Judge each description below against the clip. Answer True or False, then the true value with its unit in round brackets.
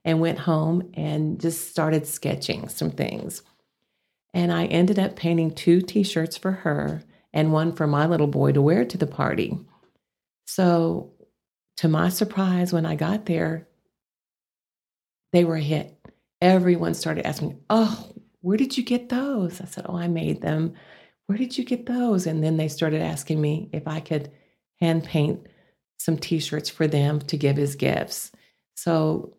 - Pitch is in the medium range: True (165 Hz)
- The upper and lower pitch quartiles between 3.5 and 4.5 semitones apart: False (2.7 semitones)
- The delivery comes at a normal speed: True (165 wpm)